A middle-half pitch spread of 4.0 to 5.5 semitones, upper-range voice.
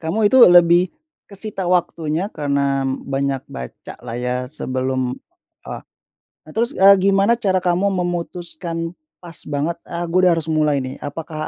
No: average, 4.3 semitones; medium, 165 Hz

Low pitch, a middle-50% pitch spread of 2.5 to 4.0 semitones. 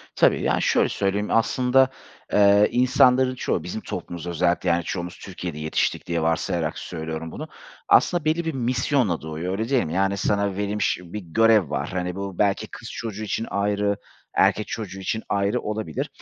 No: low, 100 Hz; average, 4.4 semitones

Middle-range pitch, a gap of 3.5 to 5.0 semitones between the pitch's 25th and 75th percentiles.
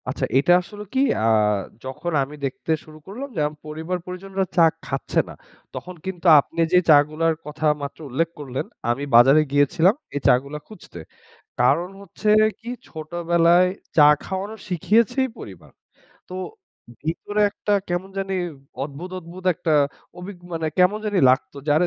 Yes: medium, 170 Hz; average, 4.0 semitones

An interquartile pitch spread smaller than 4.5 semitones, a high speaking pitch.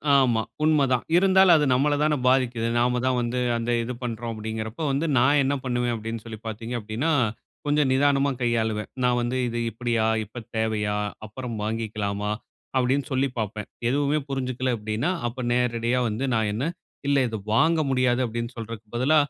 No: average, 3.2 semitones; low, 120 Hz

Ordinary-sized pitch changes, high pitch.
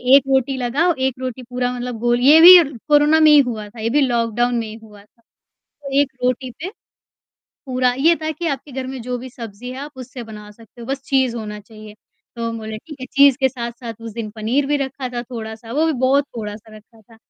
Yes: average, 3.1 semitones; very high, 250 Hz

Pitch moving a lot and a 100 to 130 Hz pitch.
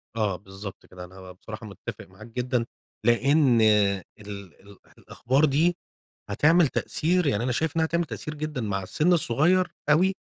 Yes: wide, 7.4 semitones; low, 125 Hz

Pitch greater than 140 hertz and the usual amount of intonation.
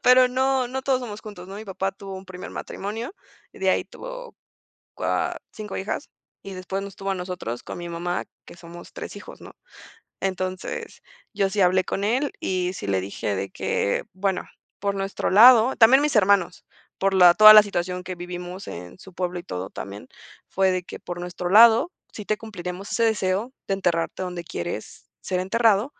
Yes: high, 190 Hz; average, 3.1 semitones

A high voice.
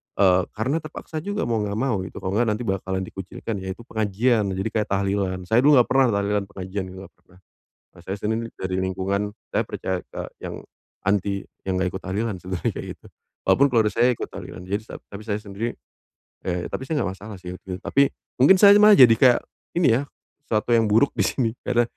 No: low, 105 Hz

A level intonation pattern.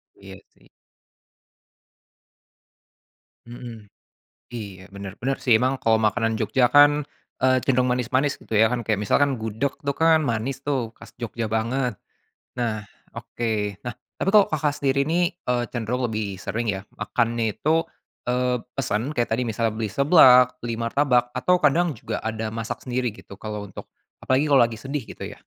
No: average, 3.3 semitones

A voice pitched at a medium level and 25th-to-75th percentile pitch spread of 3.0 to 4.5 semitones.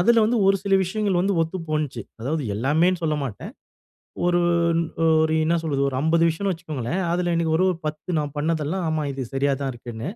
Yes: medium, 160 Hz; average, 3.9 semitones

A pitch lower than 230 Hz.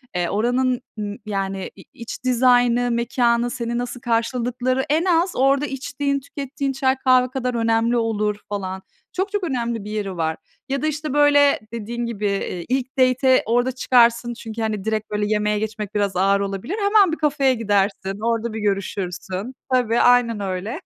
No: high, 235 Hz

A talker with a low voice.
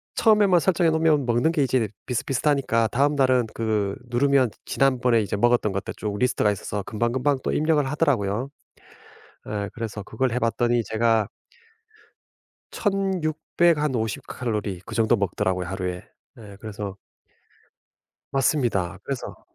Yes: low, 120 Hz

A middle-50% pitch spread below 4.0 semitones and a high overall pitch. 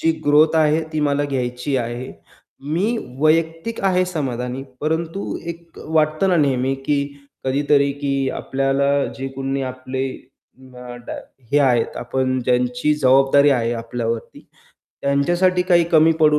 No: average, 3.5 semitones; medium, 140 Hz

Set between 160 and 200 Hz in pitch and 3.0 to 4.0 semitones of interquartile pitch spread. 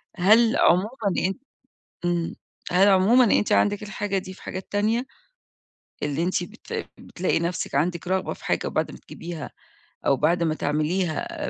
Yes: medium, 185 Hz; average, 3.3 semitones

